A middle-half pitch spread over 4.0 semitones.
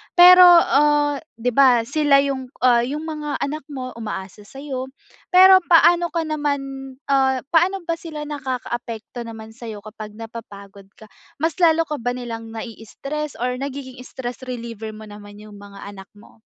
Yes: average, 4.9 semitones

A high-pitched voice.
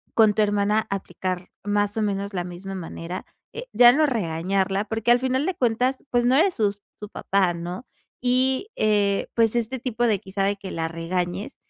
Yes: high, 205 Hz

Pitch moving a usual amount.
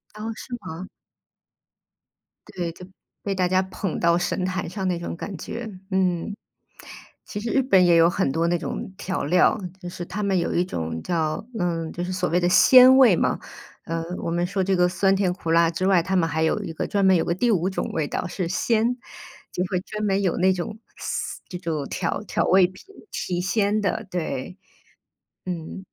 No: narrow, 2.3 semitones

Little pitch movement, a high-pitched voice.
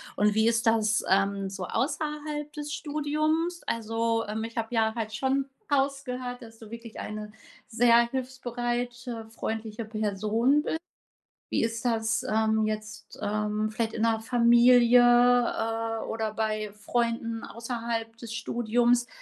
Yes: narrow, 2.0 semitones; high, 230 Hz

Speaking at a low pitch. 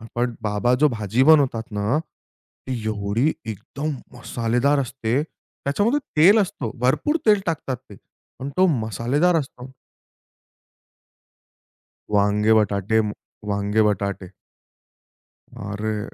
Yes: low, 120 Hz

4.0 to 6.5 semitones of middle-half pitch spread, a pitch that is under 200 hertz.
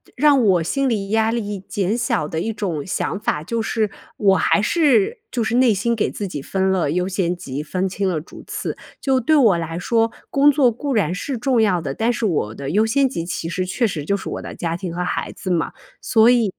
No: average, 5.0 semitones; high, 205 Hz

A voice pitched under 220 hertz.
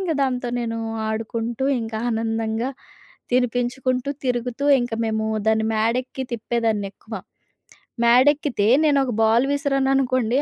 No: high, 240 Hz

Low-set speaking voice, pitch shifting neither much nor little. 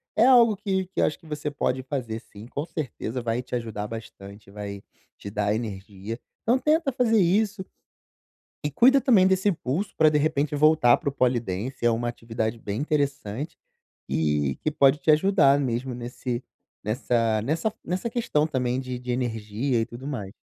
No: low, 130 Hz; wide, 5.9 semitones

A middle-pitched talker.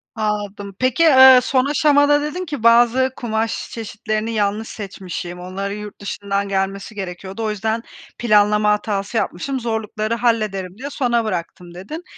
No: high, 215 Hz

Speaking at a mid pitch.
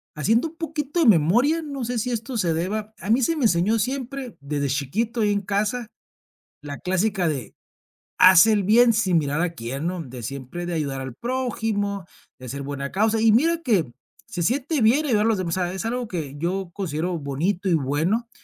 No: high, 200 Hz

